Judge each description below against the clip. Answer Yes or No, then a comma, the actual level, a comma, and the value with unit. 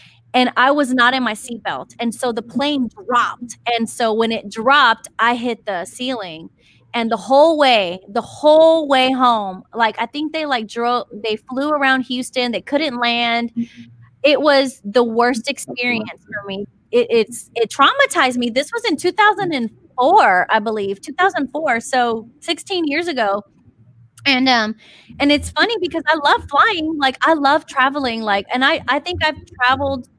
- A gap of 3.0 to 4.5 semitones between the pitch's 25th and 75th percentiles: Yes, average, 4.0 semitones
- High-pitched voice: Yes, very high, 250 Hz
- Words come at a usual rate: Yes, average, 170 wpm